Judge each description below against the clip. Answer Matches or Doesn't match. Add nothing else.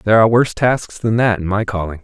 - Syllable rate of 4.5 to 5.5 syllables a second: Doesn't match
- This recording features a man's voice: Matches